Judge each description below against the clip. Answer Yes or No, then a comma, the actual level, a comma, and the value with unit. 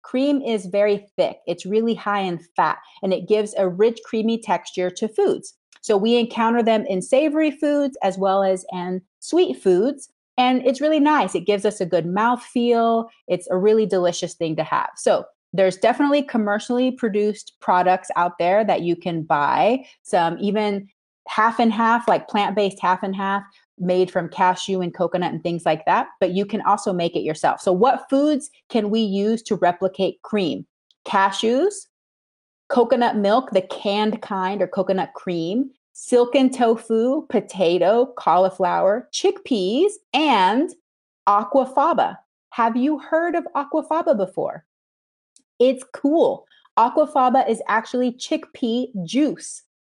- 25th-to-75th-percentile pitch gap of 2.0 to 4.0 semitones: No, wide, 5.4 semitones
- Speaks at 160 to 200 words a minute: No, average, 150 wpm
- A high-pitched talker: Yes, high, 220 Hz